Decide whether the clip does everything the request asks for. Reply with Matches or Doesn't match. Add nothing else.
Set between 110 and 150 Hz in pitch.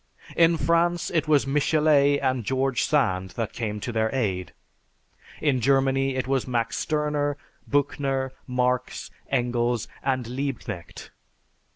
Matches